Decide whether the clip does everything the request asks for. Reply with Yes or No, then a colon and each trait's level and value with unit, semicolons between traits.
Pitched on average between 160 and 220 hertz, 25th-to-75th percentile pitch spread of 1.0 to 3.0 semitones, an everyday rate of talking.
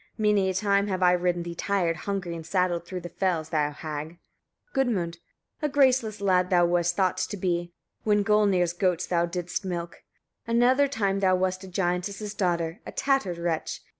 Yes: medium, 185 Hz; narrow, 2.6 semitones; average, 180 wpm